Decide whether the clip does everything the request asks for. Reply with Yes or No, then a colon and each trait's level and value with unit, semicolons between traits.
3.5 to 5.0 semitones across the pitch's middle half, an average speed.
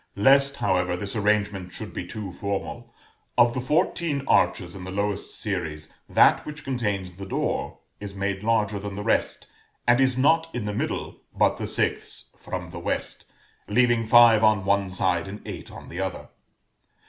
Yes: average, 3.8 semitones; average, 170 wpm